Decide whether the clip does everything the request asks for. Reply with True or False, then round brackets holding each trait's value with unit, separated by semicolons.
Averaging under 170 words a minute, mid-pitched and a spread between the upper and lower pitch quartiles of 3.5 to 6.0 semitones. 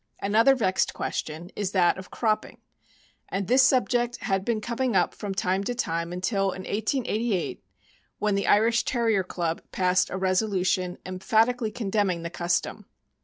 False (160 wpm; 200 Hz; 3.8 semitones)